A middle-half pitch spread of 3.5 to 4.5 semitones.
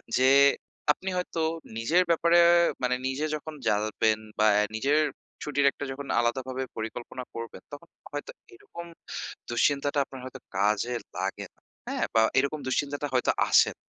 Yes: average, 3.9 semitones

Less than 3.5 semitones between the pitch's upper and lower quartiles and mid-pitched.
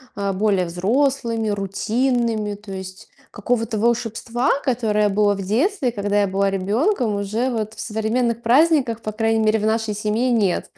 No: average, 2.8 semitones; high, 220 Hz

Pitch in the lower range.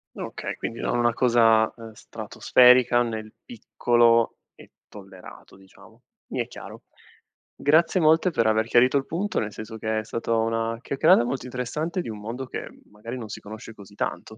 Yes: low, 115 Hz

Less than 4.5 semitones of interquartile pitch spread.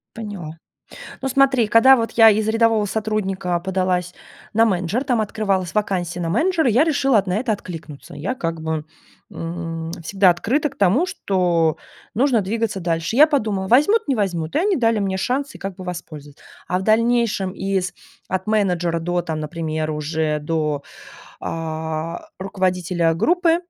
No: average, 5.3 semitones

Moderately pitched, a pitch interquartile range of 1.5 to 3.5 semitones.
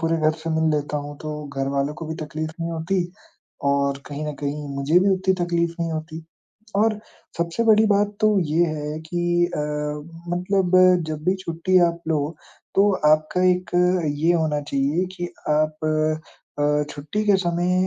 Yes: medium, 165 Hz; average, 3.1 semitones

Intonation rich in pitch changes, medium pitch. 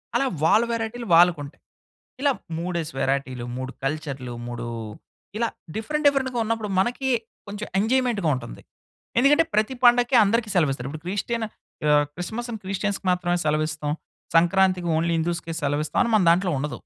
Yes: wide, 7.0 semitones; medium, 180 Hz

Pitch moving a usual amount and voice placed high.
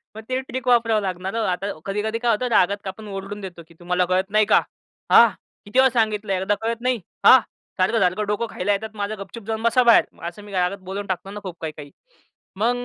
Yes: average, 3.2 semitones; high, 205 Hz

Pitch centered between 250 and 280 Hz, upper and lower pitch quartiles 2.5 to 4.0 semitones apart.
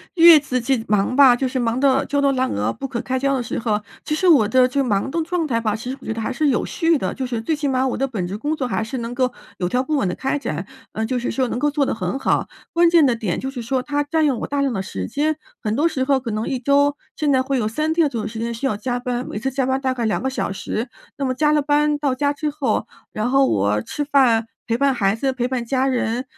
Yes: very high, 260 Hz; average, 3.7 semitones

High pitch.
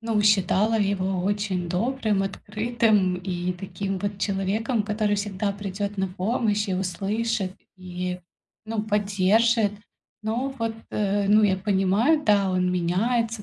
Yes: high, 205 Hz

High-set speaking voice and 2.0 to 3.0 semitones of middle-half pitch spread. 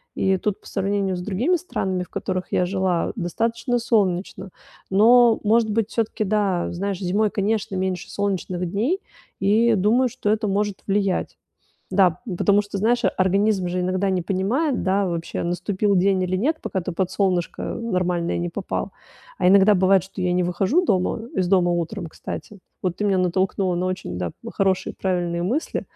Yes: high, 195 Hz; narrow, 2.5 semitones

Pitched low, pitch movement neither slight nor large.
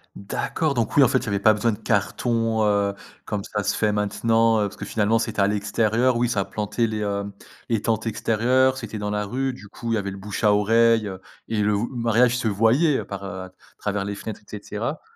No: low, 110 Hz; narrow, 2.1 semitones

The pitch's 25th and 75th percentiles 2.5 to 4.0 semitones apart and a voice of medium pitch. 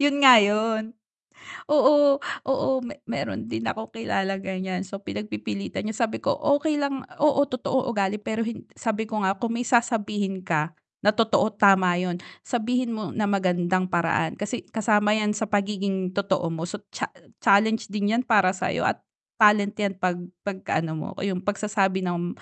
No: average, 3.3 semitones; high, 205 Hz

